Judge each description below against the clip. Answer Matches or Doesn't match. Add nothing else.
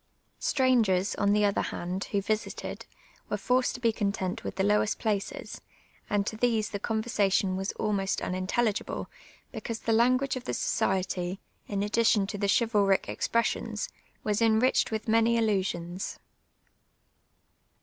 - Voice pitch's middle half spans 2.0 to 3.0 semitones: Matches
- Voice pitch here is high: Matches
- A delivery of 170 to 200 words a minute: Doesn't match